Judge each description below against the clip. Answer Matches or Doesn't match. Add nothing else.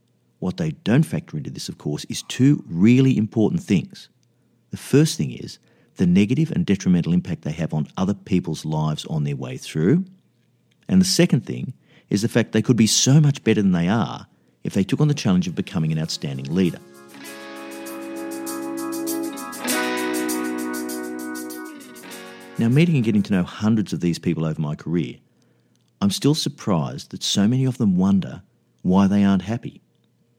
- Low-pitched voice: Matches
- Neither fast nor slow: Matches